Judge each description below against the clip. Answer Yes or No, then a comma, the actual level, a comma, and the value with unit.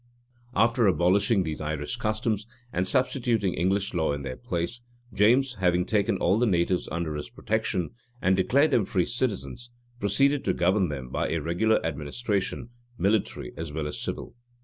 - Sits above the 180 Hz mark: No, very low, 95 Hz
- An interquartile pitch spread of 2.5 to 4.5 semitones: No, average, 5.3 semitones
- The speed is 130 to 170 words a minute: Yes, average, 165 wpm